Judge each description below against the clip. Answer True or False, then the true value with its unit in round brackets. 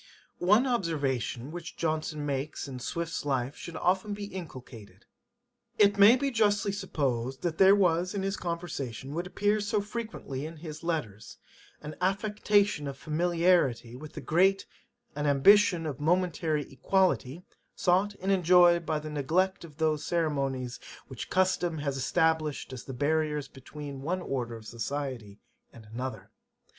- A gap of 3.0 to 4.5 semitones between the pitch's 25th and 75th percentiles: False (5.3 semitones)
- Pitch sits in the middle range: True (160 Hz)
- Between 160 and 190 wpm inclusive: False (145 wpm)